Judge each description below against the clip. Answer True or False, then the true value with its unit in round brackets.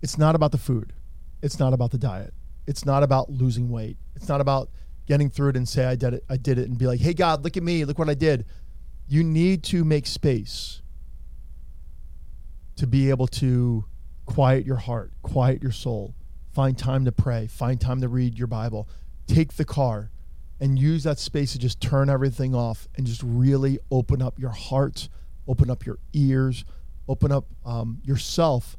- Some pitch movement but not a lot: True (3.9 semitones)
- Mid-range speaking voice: False (130 Hz)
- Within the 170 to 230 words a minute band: True (195 wpm)